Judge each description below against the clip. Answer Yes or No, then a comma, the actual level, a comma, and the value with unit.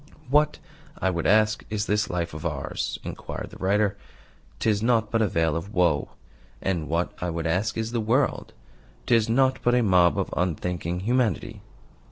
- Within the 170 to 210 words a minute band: Yes, average, 175 wpm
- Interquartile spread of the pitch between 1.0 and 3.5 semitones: No, average, 4.6 semitones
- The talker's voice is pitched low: Yes, low, 100 Hz